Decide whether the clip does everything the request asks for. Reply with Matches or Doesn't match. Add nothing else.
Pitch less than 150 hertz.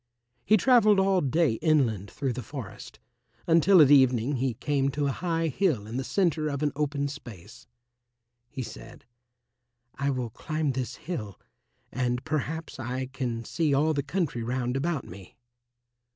Matches